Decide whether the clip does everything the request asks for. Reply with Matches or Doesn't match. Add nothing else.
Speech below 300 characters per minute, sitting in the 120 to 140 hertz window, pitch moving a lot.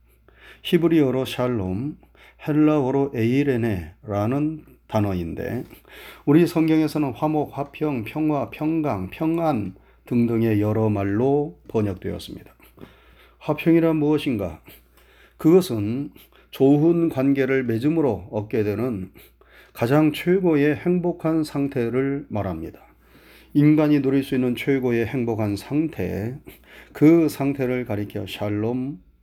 Matches